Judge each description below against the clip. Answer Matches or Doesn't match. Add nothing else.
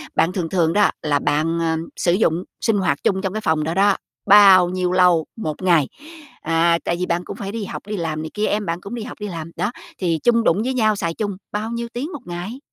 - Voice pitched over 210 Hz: Doesn't match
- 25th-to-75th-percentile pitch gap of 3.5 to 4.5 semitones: Matches